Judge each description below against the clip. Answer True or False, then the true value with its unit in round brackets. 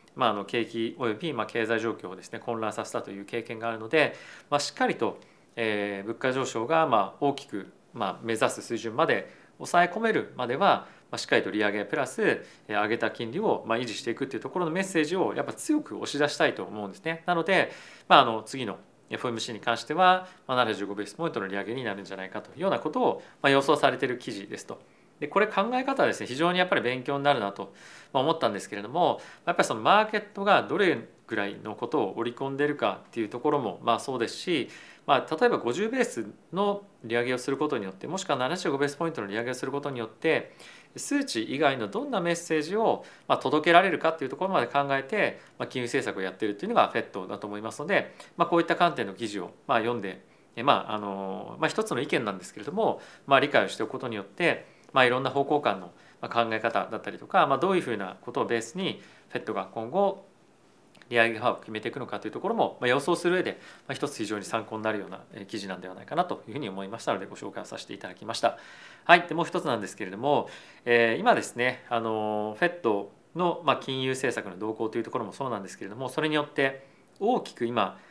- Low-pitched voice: True (130 Hz)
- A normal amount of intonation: False (7.2 semitones)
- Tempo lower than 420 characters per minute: False (465 characters per minute)